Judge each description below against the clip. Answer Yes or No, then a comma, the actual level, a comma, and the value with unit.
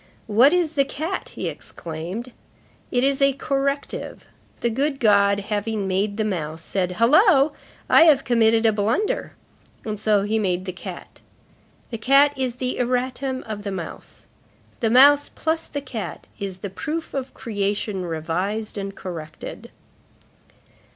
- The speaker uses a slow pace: No, average, 145 wpm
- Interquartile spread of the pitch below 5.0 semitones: No, wide, 5.4 semitones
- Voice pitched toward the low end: No, high, 225 Hz